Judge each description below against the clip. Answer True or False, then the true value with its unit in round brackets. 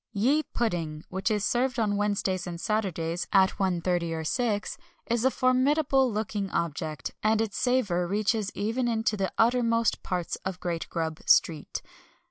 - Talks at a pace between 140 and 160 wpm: True (150 wpm)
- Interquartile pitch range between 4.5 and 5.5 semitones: True (4.8 semitones)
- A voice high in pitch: True (205 Hz)